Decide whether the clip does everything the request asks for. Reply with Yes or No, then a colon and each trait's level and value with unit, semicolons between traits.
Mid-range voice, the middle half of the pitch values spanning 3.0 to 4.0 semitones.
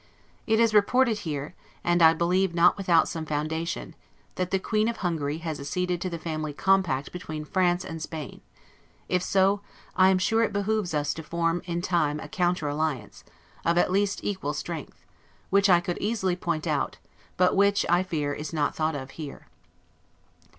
Yes: medium, 175 Hz; average, 3.4 semitones